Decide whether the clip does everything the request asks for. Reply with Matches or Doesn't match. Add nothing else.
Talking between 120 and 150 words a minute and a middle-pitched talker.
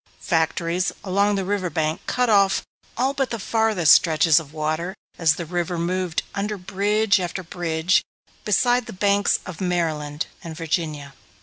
Matches